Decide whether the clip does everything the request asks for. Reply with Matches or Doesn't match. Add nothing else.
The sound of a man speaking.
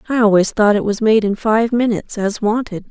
Doesn't match